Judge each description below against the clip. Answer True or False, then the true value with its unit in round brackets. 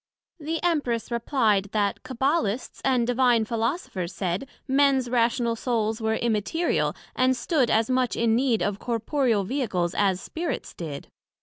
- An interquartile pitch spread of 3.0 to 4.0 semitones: True (3.4 semitones)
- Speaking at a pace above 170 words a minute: False (135 wpm)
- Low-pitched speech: False (235 Hz)